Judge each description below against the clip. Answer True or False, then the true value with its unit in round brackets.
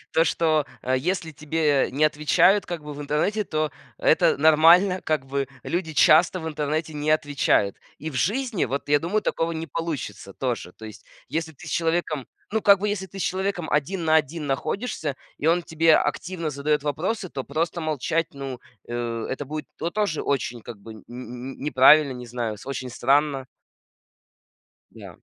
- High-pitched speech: False (155 Hz)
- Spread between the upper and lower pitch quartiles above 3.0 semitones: True (3.5 semitones)